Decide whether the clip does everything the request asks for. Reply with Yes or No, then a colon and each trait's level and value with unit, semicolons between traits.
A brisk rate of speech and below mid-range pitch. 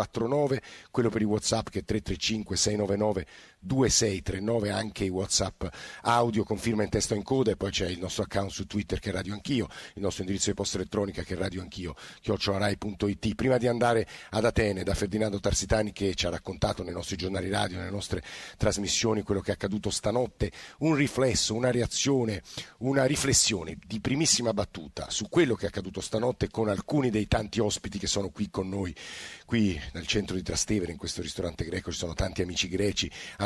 Yes: fast, 190 wpm; low, 100 Hz